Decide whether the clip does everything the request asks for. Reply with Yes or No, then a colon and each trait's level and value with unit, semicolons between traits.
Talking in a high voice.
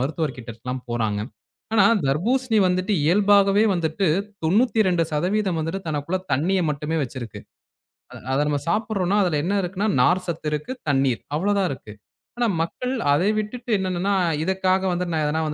No: medium, 175 Hz